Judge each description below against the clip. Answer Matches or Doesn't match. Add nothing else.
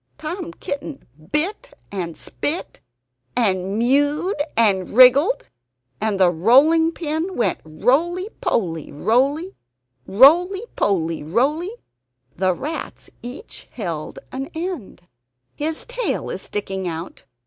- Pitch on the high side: Matches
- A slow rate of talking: Matches